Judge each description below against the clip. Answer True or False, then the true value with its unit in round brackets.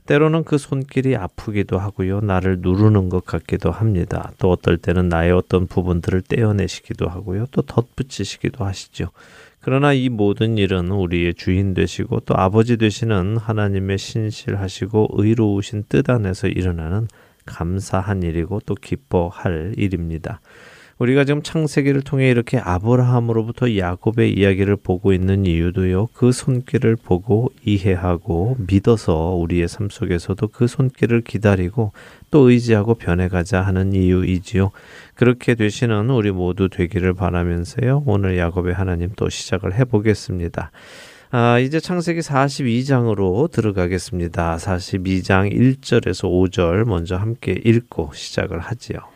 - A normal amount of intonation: True (4.4 semitones)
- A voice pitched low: True (100 Hz)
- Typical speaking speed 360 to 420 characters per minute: False (325 characters per minute)